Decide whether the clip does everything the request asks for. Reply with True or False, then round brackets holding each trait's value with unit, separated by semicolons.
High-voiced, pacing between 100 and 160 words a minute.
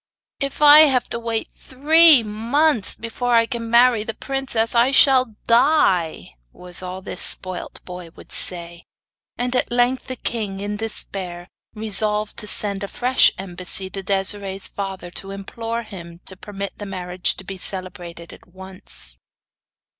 True (210 Hz; 155 wpm)